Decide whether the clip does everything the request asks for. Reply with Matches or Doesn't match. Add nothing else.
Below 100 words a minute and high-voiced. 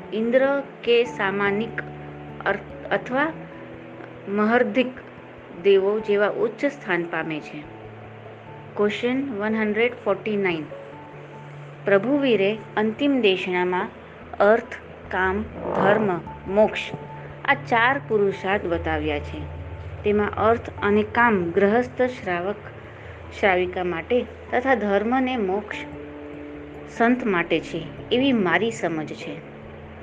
Matches